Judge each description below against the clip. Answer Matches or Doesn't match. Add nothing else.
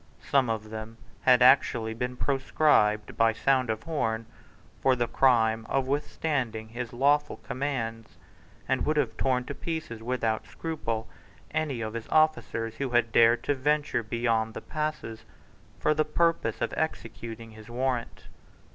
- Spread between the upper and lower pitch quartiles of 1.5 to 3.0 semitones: Doesn't match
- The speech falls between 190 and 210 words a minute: Doesn't match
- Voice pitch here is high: Doesn't match